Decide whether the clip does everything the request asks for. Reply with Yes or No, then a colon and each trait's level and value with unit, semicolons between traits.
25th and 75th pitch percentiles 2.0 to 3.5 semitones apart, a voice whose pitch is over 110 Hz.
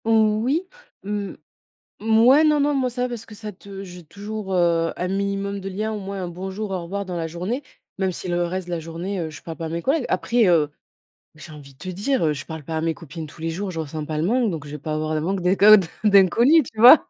No: average, 4.5 semitones; high, 190 Hz